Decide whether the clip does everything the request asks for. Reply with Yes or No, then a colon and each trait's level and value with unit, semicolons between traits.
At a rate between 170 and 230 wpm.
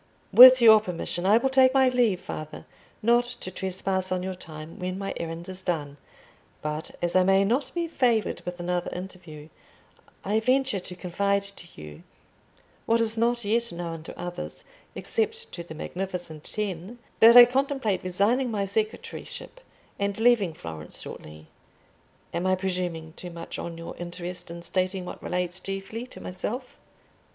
No: average, 155 wpm